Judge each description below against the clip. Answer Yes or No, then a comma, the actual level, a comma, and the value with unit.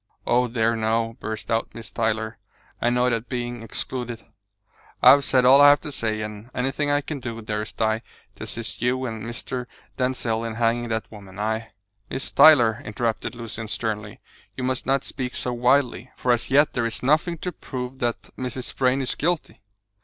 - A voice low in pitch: Yes, low, 120 Hz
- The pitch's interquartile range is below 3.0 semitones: Yes, narrow, 2.5 semitones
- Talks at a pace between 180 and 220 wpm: Yes, average, 185 wpm